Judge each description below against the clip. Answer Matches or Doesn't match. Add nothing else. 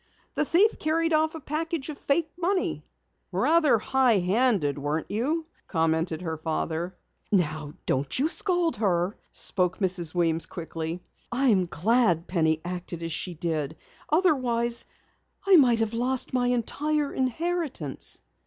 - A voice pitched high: Matches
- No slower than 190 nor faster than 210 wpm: Doesn't match